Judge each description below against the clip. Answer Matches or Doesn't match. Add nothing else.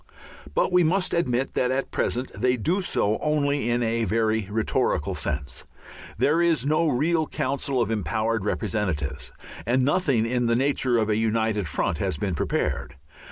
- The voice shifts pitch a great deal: Doesn't match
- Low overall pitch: Matches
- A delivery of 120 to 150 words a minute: Doesn't match